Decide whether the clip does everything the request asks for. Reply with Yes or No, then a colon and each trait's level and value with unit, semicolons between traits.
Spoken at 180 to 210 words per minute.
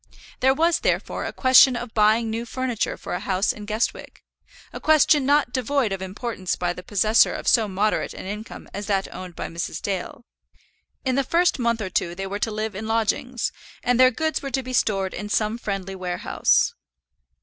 Yes: average, 195 wpm